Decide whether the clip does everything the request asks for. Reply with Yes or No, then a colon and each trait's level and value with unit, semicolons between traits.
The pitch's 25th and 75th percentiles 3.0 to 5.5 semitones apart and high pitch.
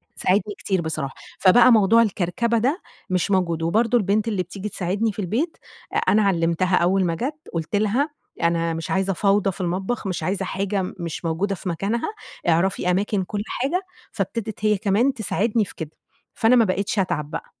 Yes: average, 3.5 semitones; high, 195 Hz